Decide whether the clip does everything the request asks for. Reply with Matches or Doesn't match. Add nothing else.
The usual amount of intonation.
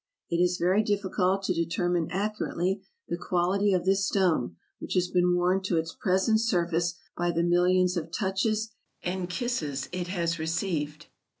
Doesn't match